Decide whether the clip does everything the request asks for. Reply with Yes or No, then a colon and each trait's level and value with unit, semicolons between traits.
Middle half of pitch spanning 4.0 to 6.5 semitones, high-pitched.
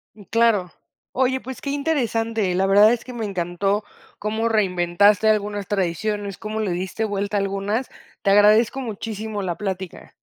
No: narrow, 2.4 semitones; high, 210 Hz